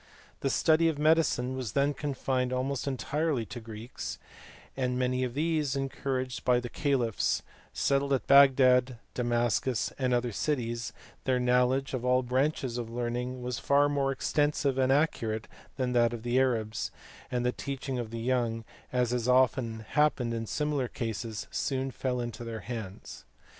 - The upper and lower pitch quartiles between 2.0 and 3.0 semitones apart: Yes, narrow, 2.4 semitones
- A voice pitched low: Yes, low, 125 Hz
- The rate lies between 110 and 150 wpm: No, average, 160 wpm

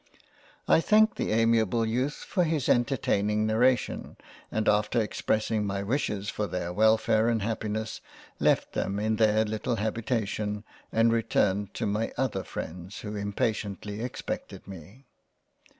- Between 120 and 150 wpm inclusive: Yes, slow, 135 wpm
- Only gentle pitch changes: Yes, narrow, 2.0 semitones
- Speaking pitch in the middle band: No, low, 110 Hz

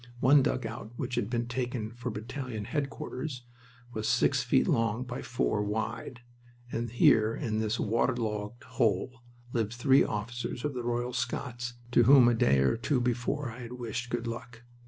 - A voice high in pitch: No, low, 120 Hz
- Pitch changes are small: Yes, narrow, 2.0 semitones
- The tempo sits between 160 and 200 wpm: Yes, average, 165 wpm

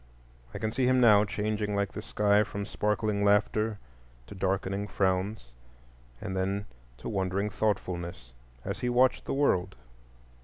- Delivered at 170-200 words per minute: No, average, 145 wpm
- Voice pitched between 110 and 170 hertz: No, low, 100 Hz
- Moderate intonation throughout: No, narrow, 2.0 semitones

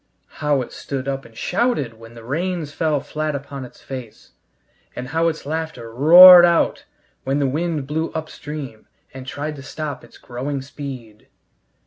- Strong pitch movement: No, average, 3.5 semitones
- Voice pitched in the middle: Yes, medium, 145 Hz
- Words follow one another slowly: No, average, 160 wpm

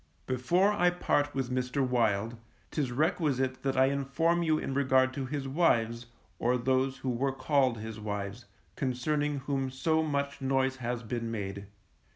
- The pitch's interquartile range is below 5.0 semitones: Yes, narrow, 2.6 semitones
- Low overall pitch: Yes, low, 130 Hz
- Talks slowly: No, average, 160 wpm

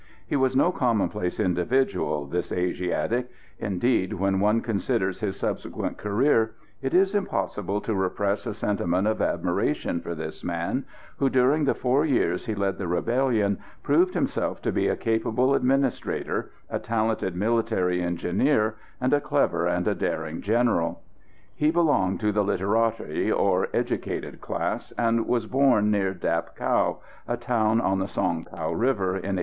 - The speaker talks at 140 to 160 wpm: Yes, average, 155 wpm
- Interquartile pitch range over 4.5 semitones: Yes, average, 5.1 semitones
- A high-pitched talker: No, low, 105 Hz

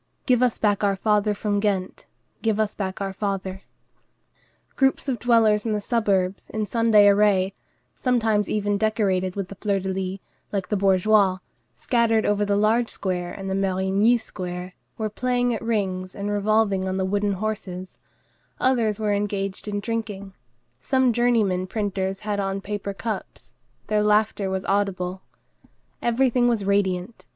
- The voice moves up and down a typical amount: No, narrow, 2.2 semitones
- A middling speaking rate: Yes, average, 155 wpm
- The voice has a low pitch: No, high, 205 Hz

